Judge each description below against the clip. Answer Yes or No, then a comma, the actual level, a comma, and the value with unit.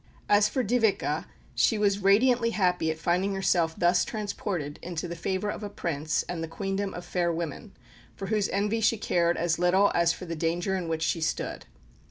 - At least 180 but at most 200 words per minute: Yes, average, 195 wpm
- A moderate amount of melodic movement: Yes, average, 3.3 semitones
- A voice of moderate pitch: Yes, medium, 180 Hz